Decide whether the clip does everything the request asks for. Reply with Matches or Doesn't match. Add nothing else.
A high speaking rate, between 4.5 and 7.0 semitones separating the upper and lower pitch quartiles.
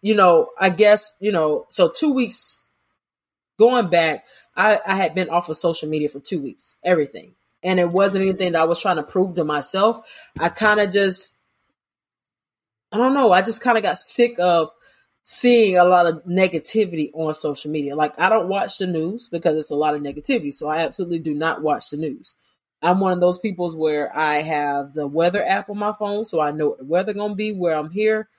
Matches